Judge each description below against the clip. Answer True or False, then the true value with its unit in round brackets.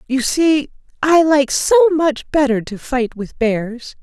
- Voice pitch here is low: False (275 Hz)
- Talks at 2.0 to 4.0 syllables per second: True (3.6 syllables/s)